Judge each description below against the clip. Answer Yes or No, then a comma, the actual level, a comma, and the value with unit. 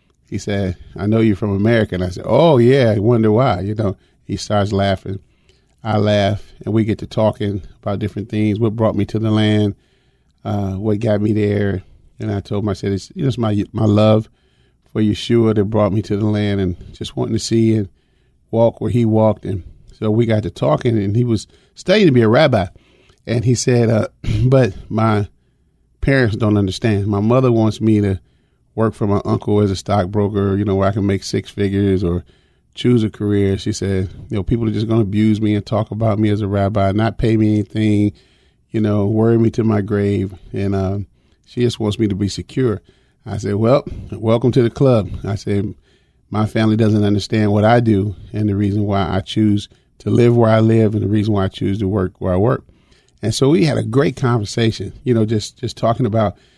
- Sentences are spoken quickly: Yes, fast, 220 wpm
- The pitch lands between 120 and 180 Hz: No, low, 105 Hz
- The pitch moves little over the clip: Yes, narrow, 2.0 semitones